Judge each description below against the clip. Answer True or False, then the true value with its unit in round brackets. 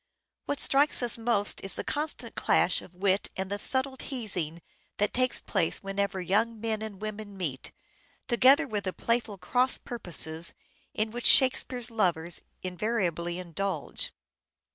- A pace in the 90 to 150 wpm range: True (145 wpm)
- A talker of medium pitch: False (210 Hz)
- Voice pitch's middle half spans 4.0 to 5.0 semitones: True (4.4 semitones)